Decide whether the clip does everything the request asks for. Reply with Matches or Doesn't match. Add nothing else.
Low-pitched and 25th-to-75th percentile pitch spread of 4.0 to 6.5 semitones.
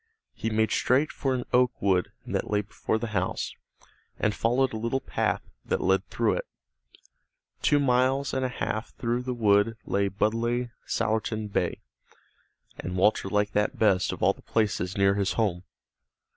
Doesn't match